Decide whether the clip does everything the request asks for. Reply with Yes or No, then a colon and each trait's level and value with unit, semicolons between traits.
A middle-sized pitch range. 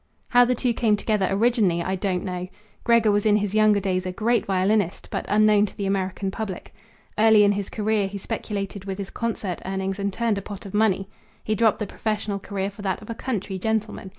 No: narrow, 2.0 semitones